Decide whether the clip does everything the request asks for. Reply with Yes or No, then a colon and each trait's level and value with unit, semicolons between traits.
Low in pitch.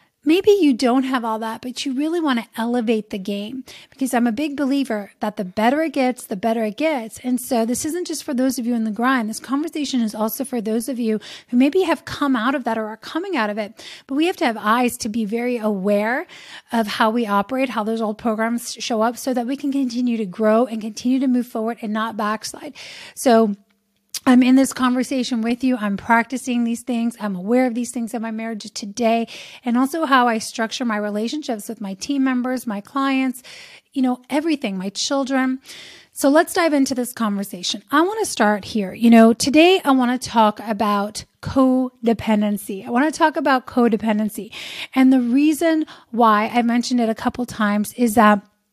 No: high, 240 Hz